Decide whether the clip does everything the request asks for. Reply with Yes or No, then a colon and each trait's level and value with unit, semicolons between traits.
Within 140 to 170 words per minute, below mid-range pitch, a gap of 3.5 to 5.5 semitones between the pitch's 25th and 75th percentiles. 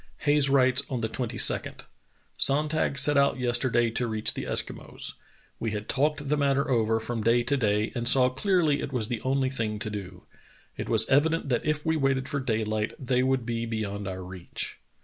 No: average, 190 wpm; low, 125 Hz; average, 3.8 semitones